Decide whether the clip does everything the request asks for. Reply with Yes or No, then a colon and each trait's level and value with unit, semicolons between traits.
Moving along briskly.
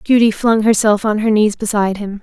Yes: fast, 215 wpm